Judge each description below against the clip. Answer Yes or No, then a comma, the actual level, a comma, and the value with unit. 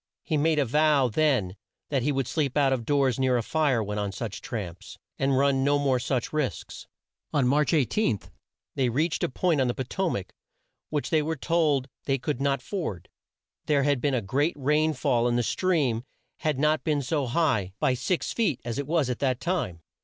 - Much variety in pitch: No, average, 3.7 semitones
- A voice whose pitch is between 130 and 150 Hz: Yes, medium, 140 Hz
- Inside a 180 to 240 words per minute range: Yes, fast, 205 wpm